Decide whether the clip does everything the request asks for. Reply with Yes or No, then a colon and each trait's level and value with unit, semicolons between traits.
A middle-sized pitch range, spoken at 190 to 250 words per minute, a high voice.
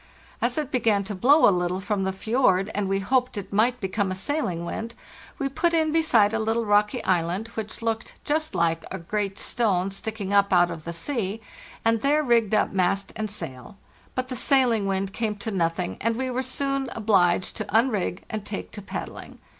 Yes: average, 4.0 semitones; average, 200 wpm; high, 210 Hz